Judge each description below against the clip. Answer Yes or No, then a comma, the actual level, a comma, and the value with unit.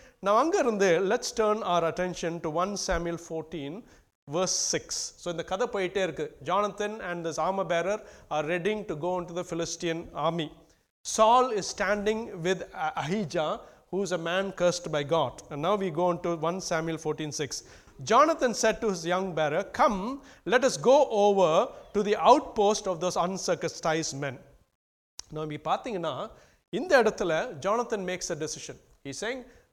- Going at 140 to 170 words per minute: Yes, average, 155 wpm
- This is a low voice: No, medium, 180 Hz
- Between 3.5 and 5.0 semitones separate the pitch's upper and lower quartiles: Yes, average, 4.2 semitones